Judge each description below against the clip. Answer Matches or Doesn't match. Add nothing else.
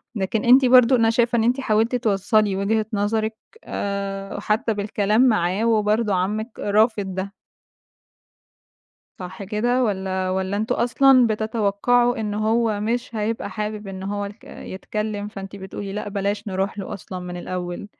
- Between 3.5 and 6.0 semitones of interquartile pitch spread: Doesn't match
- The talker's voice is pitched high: Matches